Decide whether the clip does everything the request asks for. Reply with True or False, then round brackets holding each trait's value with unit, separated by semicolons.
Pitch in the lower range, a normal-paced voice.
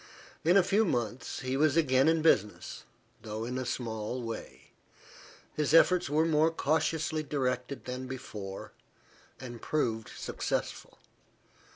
False (130 Hz; 130 wpm)